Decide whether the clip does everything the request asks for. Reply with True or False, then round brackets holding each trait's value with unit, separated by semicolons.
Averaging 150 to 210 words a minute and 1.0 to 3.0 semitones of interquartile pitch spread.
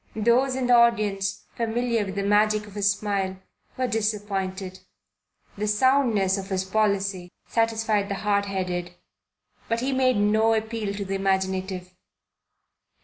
False (140 wpm; 2.6 semitones)